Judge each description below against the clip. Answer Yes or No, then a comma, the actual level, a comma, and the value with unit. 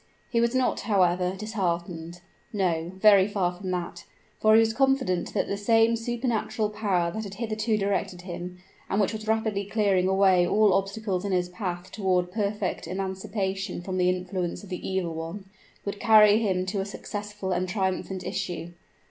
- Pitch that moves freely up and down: No, average, 2.9 semitones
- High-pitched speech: Yes, high, 195 Hz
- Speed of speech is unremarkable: Yes, average, 170 wpm